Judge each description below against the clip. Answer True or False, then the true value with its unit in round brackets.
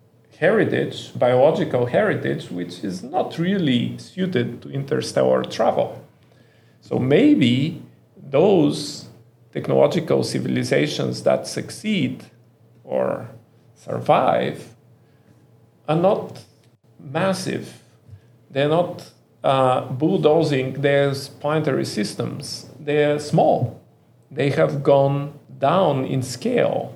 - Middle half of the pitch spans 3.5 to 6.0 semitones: True (4.1 semitones)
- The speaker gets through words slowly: True (85 wpm)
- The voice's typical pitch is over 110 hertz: True (140 Hz)